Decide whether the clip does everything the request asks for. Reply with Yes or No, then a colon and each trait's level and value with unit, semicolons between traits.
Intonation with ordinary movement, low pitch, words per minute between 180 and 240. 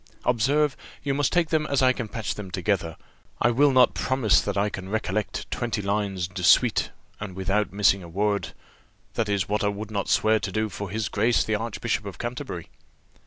Yes: average, 3.3 semitones; low, 105 Hz; average, 200 wpm